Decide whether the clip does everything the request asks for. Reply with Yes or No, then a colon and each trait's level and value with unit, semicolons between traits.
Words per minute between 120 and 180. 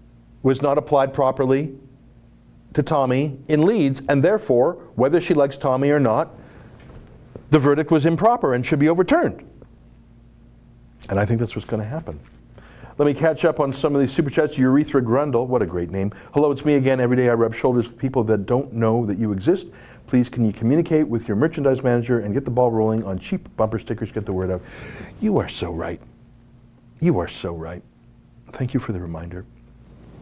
No: average, 195 wpm